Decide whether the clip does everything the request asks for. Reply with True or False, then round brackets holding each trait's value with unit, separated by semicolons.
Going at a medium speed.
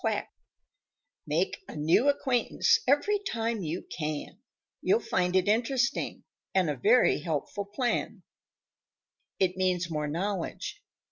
False (120 wpm)